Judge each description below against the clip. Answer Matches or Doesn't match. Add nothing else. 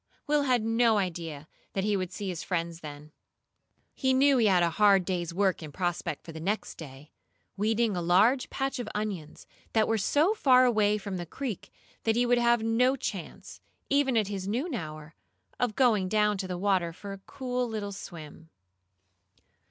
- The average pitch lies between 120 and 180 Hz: Doesn't match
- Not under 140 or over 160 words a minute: Doesn't match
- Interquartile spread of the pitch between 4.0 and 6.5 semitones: Matches